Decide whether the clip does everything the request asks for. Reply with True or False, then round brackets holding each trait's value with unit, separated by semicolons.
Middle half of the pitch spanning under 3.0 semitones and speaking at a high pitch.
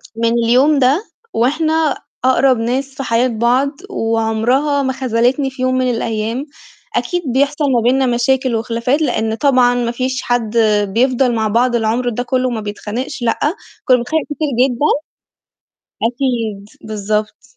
True (2.6 semitones; 245 Hz)